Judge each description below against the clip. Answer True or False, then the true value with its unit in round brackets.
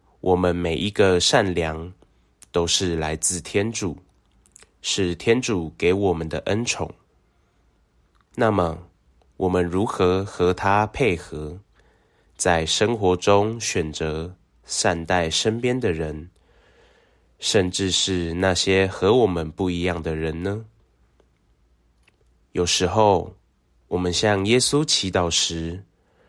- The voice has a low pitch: True (90 Hz)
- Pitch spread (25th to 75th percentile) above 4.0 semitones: False (3.5 semitones)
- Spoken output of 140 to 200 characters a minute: True (160 characters per minute)